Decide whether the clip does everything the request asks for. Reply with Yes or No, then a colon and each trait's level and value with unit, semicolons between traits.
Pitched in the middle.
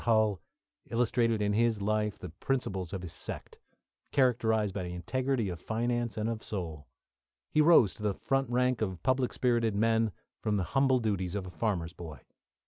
No: low, 110 Hz